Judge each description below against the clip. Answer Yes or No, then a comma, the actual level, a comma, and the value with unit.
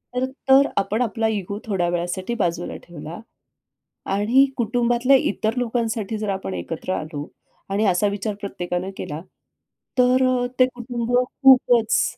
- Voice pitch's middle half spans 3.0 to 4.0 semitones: No, average, 4.7 semitones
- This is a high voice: Yes, high, 215 Hz